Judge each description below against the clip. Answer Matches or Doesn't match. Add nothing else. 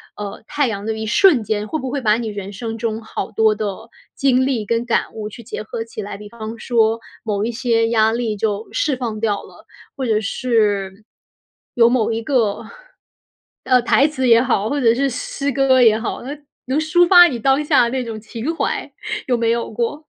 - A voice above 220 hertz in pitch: Matches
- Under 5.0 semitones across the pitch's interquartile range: Matches